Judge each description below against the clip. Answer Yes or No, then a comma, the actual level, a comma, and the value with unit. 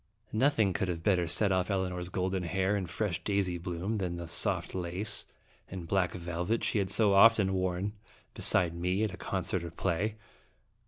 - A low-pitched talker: Yes, very low, 95 Hz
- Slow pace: No, average, 170 wpm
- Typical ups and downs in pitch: No, narrow, 2.2 semitones